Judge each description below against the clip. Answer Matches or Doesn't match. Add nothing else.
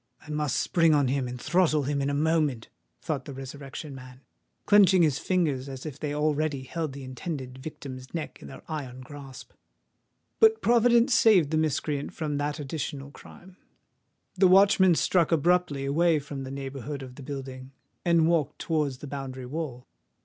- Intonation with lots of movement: Doesn't match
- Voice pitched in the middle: Matches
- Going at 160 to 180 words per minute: Matches